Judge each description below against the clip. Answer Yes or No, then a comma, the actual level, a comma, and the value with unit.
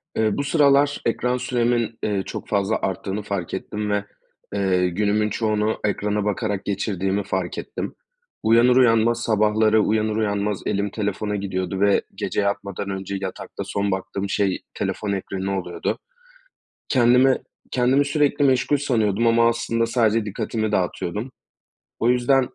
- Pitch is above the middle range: No, low, 105 Hz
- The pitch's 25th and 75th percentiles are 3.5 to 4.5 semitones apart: No, average, 2.9 semitones